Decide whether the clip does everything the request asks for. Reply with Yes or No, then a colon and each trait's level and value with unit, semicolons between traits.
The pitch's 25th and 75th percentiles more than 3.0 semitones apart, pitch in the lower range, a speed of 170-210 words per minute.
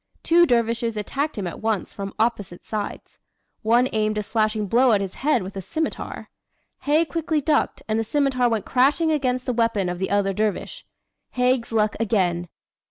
No: average, 3.9 semitones; high, 225 Hz; average, 175 wpm